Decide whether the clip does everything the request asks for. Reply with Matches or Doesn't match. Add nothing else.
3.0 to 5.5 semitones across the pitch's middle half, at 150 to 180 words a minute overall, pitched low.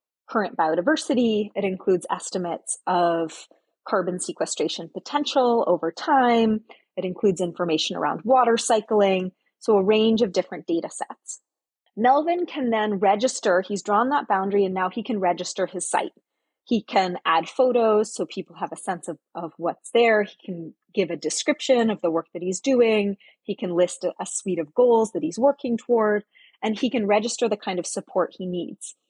Doesn't match